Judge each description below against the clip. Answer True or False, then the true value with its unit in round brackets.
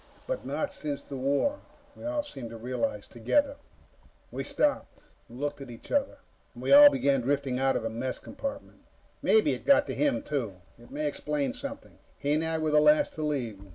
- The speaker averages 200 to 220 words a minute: True (205 wpm)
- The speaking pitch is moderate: True (145 Hz)